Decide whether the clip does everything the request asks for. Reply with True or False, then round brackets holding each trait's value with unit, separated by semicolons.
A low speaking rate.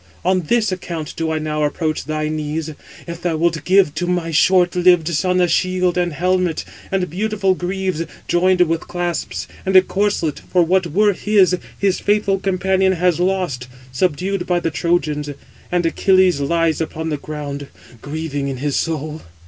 False (170 wpm)